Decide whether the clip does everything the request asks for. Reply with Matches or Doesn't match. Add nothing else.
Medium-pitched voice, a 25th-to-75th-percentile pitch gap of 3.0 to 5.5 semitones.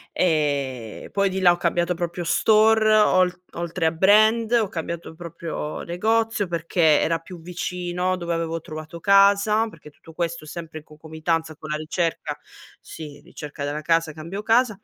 Matches